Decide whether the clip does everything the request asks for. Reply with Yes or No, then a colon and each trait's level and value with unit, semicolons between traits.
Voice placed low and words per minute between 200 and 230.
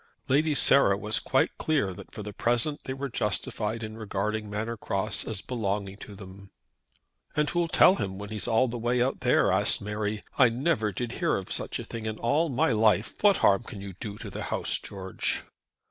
Yes: low, 110 Hz; fast, 205 wpm